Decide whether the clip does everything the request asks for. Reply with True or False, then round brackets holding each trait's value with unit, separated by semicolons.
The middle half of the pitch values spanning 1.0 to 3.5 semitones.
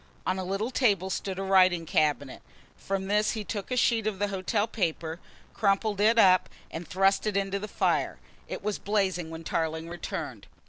True (2.8 semitones)